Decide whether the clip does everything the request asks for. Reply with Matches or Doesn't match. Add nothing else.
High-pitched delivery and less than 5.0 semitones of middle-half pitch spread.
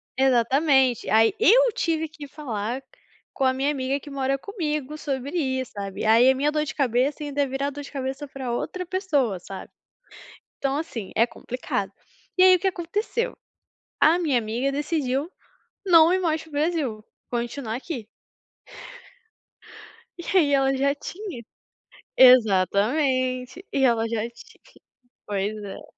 Matches